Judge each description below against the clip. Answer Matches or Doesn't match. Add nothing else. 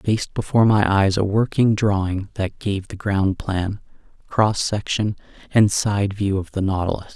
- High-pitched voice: Doesn't match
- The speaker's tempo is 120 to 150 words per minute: Doesn't match